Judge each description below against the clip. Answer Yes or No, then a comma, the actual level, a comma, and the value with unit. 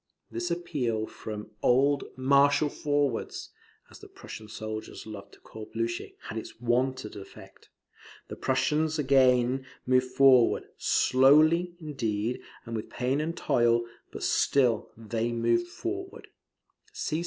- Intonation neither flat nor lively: Yes, average, 3.8 semitones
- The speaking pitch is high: No, low, 130 Hz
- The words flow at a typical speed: No, slow, 120 wpm